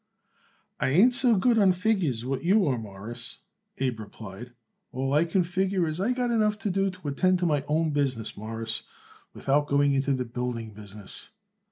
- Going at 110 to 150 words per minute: No, average, 180 wpm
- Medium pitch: Yes, medium, 145 Hz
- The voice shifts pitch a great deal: Yes, wide, 7.7 semitones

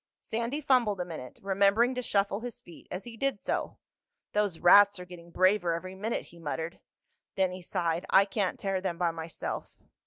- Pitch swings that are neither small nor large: Yes, average, 3.3 semitones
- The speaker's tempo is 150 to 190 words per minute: Yes, average, 185 wpm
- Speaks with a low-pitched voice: No, high, 190 Hz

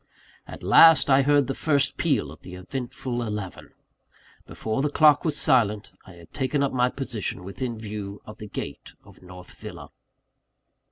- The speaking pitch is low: Yes, low, 120 Hz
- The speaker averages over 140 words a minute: Yes, average, 165 wpm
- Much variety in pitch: Yes, wide, 5.7 semitones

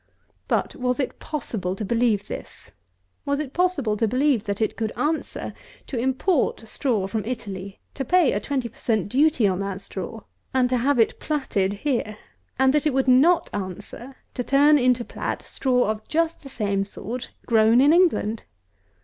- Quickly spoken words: No, average, 175 wpm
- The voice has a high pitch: Yes, high, 245 Hz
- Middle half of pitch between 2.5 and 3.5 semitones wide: No, average, 4.8 semitones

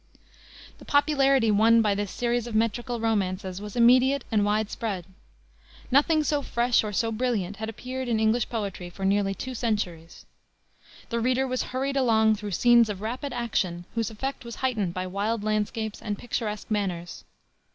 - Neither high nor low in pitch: No, high, 225 Hz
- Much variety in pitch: No, average, 3.2 semitones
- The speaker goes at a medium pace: Yes, average, 165 wpm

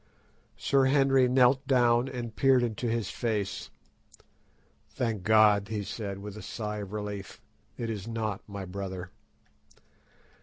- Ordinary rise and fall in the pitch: Yes, average, 3.4 semitones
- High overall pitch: No, low, 110 Hz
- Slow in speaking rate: Yes, slow, 130 wpm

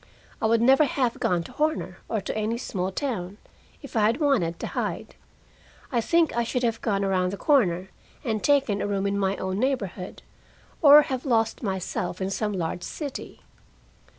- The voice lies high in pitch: Yes, high, 220 Hz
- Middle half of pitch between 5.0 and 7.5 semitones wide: Yes, wide, 5.4 semitones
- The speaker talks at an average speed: Yes, average, 180 wpm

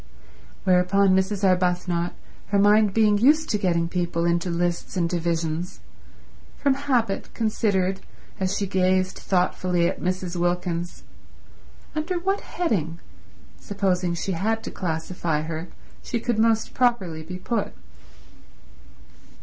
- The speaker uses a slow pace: Yes, slow, 120 wpm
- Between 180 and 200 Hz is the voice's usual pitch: Yes, medium, 185 Hz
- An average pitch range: Yes, average, 3.4 semitones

